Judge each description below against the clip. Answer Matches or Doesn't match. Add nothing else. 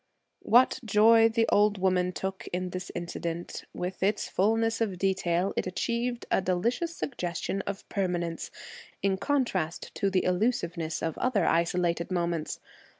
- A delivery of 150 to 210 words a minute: Doesn't match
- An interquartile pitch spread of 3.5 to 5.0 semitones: Matches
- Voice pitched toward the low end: Doesn't match